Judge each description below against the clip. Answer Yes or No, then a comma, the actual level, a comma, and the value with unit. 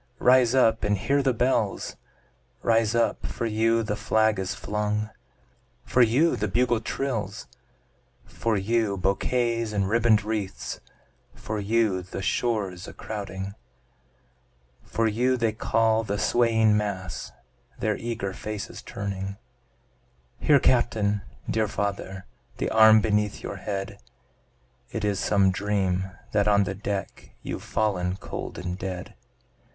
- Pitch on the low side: Yes, low, 105 Hz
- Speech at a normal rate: No, slow, 130 wpm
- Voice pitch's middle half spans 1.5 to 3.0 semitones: Yes, narrow, 2.5 semitones